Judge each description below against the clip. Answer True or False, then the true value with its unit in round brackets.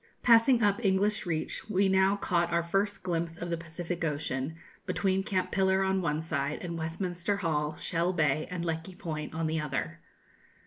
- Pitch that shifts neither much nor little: True (3.1 semitones)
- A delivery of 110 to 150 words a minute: False (175 wpm)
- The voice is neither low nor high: True (170 Hz)